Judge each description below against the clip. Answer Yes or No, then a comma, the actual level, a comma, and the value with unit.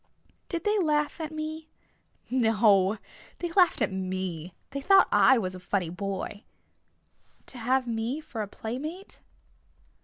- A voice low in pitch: No, high, 240 Hz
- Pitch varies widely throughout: Yes, wide, 8.0 semitones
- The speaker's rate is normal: Yes, average, 145 wpm